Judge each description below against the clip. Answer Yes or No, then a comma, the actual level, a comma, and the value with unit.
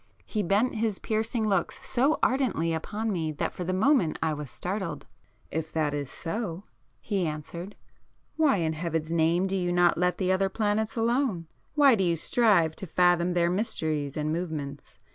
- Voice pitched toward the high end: No, medium, 180 Hz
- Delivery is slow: No, average, 175 wpm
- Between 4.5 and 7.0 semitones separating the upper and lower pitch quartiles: Yes, average, 5.0 semitones